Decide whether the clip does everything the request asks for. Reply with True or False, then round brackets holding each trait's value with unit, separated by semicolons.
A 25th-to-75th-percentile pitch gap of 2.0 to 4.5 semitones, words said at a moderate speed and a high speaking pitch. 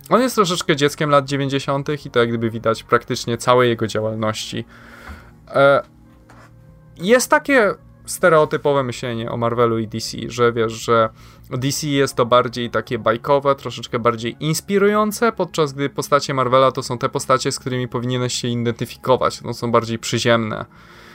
False (3.4 semitones; 145 wpm; 125 Hz)